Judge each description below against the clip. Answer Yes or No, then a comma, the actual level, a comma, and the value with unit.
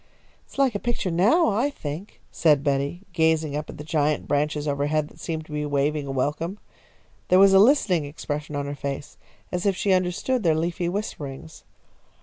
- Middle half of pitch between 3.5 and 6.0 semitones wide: Yes, average, 4.4 semitones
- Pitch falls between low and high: Yes, medium, 160 Hz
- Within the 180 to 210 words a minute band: Yes, average, 190 wpm